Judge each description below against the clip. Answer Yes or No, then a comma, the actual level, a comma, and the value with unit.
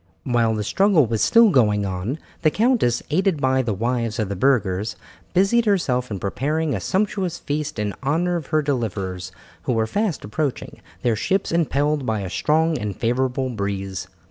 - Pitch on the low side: Yes, low, 130 Hz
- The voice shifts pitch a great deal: Yes, wide, 7.0 semitones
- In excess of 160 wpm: Yes, average, 170 wpm